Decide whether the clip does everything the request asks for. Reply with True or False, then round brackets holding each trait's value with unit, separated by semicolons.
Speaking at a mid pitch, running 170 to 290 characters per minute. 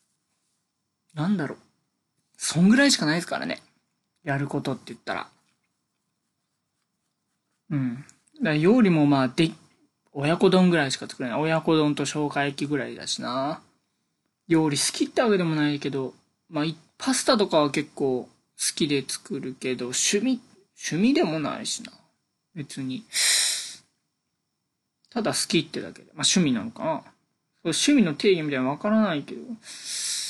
True (155 Hz; 280 characters per minute)